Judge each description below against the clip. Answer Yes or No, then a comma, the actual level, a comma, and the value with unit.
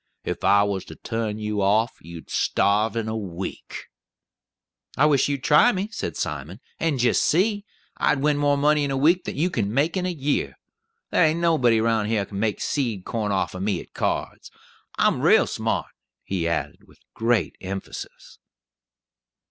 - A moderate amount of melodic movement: No, wide, 6.5 semitones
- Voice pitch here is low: Yes, low, 115 Hz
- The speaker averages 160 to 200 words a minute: Yes, average, 180 wpm